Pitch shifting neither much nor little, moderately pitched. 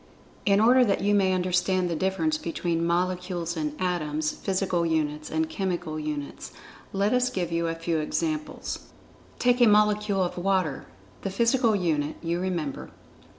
Yes: average, 3.6 semitones; medium, 180 Hz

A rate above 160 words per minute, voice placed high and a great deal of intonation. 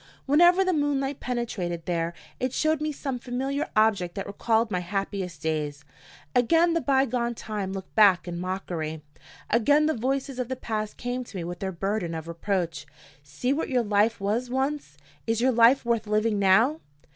Yes: average, 180 wpm; high, 225 Hz; wide, 6.1 semitones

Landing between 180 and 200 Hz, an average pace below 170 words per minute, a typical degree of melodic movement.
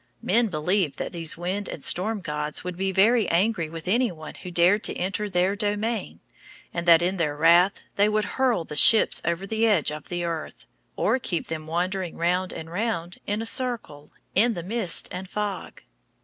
No: medium, 185 Hz; average, 190 wpm; average, 3.8 semitones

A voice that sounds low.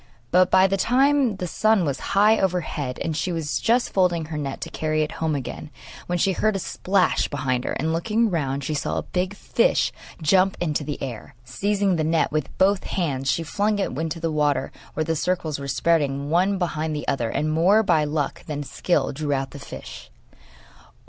No: medium, 165 Hz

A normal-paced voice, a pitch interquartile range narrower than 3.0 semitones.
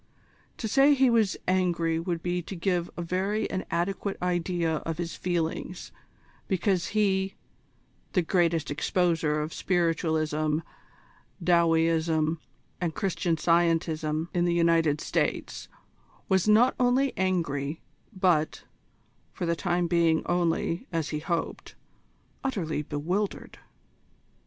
No: slow, 115 wpm; narrow, 2.4 semitones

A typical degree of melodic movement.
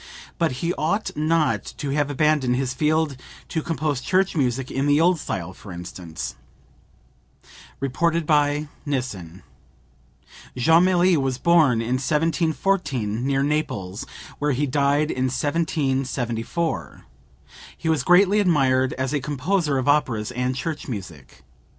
Yes: average, 4.0 semitones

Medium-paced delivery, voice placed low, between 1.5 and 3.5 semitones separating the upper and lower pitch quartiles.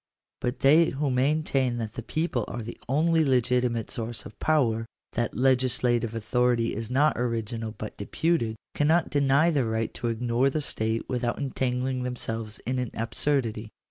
Yes: average, 170 wpm; low, 125 Hz; average, 3.1 semitones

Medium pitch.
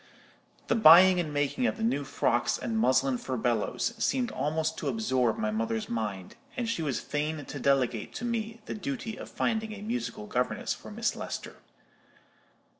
Yes: medium, 150 Hz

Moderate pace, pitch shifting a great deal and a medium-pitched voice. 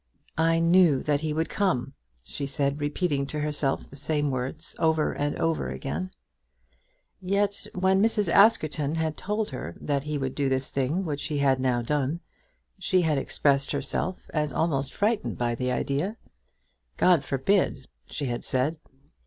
No: average, 160 wpm; average, 3.5 semitones; medium, 150 Hz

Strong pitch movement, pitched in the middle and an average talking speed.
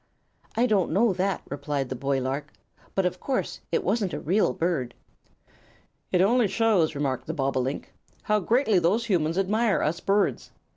Yes: wide, 6.3 semitones; medium, 180 Hz; average, 160 wpm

